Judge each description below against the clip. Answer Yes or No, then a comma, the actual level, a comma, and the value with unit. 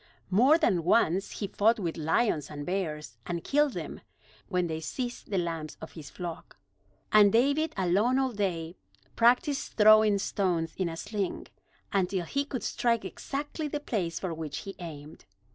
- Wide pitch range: Yes, wide, 6.0 semitones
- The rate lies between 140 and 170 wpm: Yes, average, 160 wpm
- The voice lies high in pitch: Yes, high, 195 Hz